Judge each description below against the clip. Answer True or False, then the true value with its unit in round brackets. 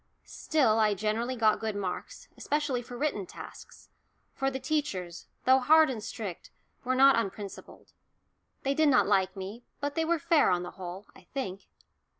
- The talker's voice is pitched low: False (240 Hz)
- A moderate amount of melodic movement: False (5.9 semitones)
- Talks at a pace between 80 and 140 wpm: False (165 wpm)